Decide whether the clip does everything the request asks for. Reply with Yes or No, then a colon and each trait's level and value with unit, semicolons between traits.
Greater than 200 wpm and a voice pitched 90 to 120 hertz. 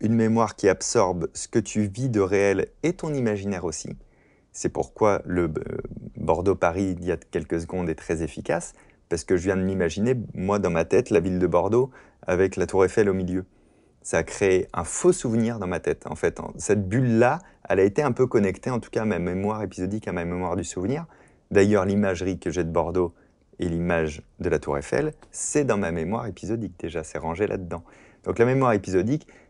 Yes: average, 210 wpm; low, 100 Hz